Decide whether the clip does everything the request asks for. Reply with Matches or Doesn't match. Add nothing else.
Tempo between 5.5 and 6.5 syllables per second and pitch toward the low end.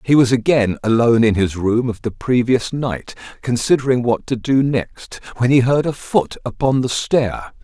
Doesn't match